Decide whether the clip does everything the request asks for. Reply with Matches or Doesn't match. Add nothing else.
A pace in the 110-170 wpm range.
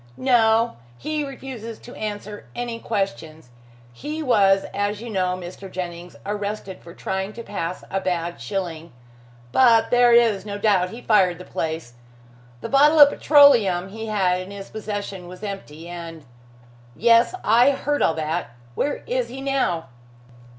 Matches